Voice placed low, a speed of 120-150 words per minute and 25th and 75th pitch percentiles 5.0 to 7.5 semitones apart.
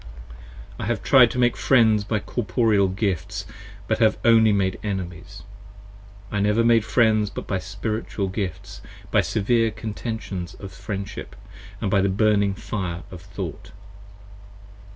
No: low, 105 Hz; slow, 135 wpm; average, 2.7 semitones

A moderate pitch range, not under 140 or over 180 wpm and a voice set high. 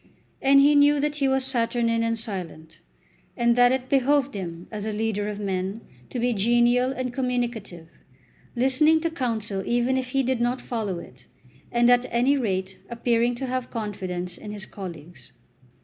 Yes: average, 4.0 semitones; average, 170 wpm; high, 235 Hz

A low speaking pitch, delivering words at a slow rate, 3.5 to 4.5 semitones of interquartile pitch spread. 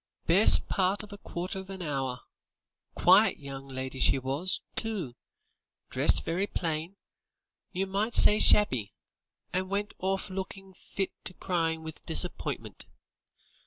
No: medium, 185 Hz; slow, 130 wpm; average, 4.1 semitones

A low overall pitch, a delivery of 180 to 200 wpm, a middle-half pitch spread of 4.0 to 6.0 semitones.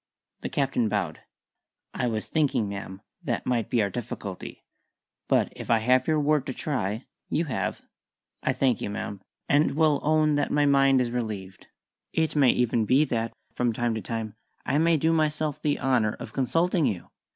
Yes: low, 130 Hz; average, 185 wpm; average, 5.1 semitones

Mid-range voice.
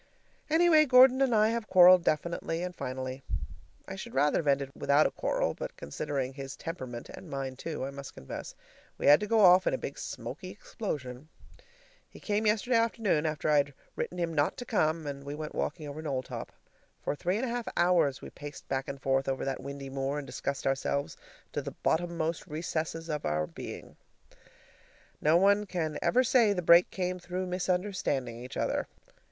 Yes: medium, 160 Hz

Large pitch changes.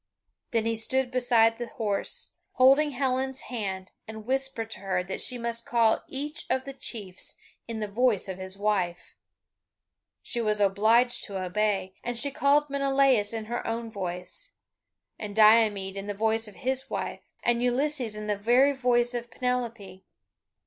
No: average, 3.6 semitones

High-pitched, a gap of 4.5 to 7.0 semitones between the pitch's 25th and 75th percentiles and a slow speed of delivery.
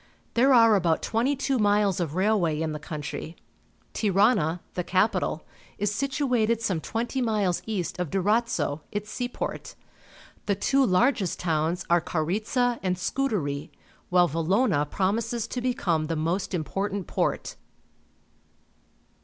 Yes: high, 195 Hz; average, 5.2 semitones; slow, 130 wpm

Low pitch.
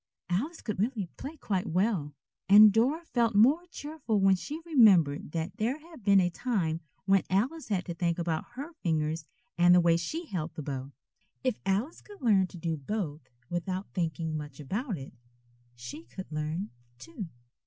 No: high, 190 Hz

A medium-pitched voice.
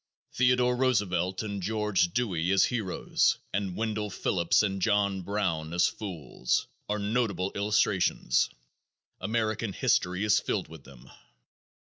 No: low, 100 Hz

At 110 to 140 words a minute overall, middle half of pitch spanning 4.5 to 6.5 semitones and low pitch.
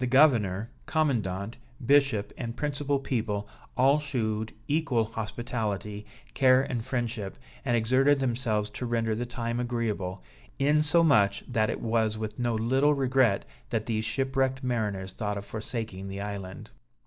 No: slow, 135 wpm; average, 3.8 semitones; low, 115 Hz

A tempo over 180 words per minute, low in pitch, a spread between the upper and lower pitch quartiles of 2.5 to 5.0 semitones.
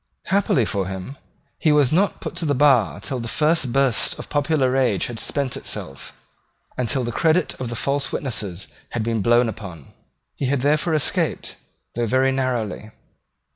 No: average, 175 wpm; low, 130 Hz; average, 4.1 semitones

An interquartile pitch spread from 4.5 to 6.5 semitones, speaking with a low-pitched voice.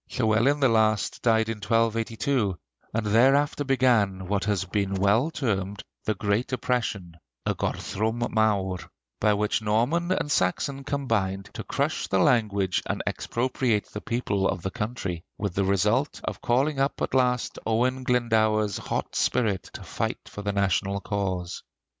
No: average, 3.9 semitones; low, 110 Hz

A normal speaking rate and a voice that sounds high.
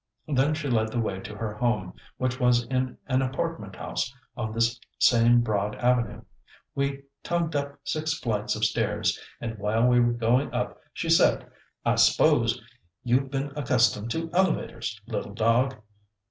No: average, 160 wpm; low, 120 Hz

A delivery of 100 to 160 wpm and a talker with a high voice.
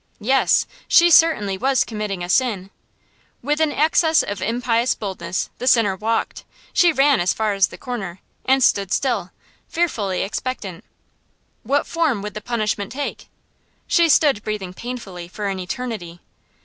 Yes: average, 150 wpm; high, 220 Hz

